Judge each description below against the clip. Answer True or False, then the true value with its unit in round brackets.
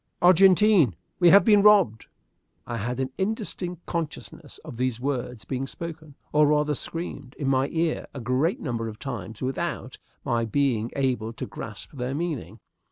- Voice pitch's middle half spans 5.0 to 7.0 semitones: True (5.3 semitones)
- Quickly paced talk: False (160 wpm)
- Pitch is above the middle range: False (140 Hz)